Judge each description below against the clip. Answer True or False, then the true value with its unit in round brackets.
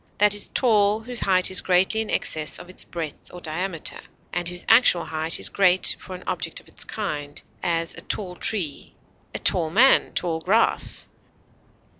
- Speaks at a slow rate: False (175 wpm)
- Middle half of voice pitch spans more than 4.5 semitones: False (3.8 semitones)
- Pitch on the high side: False (180 Hz)